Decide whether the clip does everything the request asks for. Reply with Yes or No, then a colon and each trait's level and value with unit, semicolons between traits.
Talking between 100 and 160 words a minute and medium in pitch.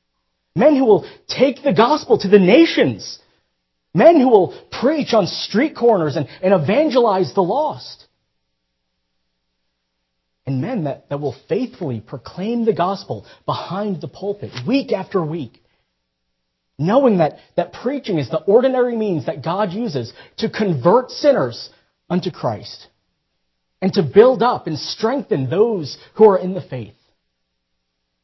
Yes: slow, 135 wpm; medium, 170 Hz